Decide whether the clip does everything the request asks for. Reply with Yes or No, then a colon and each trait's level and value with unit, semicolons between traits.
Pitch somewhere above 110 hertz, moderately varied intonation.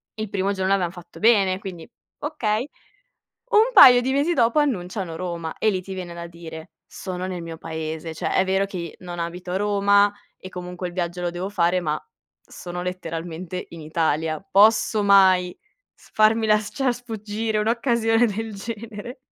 Yes: high, 190 Hz; average, 3.8 semitones